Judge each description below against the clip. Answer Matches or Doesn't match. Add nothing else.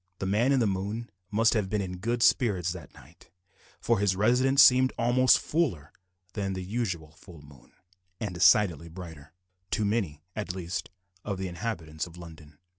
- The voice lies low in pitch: Matches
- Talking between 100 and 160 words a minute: Doesn't match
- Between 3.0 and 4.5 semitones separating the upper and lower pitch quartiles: Doesn't match